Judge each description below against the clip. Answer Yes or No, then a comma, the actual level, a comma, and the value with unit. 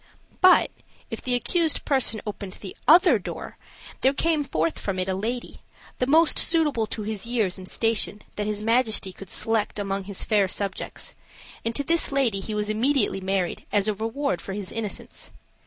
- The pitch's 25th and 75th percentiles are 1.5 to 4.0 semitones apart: No, average, 4.7 semitones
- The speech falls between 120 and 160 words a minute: No, average, 180 wpm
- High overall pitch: Yes, high, 215 Hz